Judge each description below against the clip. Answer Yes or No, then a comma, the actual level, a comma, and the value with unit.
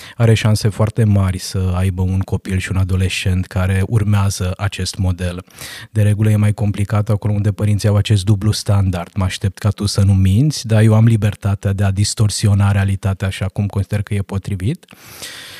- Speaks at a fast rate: Yes, fast, 185 wpm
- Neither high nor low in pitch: No, low, 100 Hz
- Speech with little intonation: Yes, narrow, 1.9 semitones